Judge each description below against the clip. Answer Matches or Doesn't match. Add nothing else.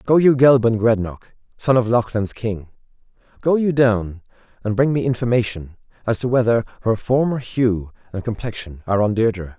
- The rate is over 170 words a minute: Doesn't match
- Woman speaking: Doesn't match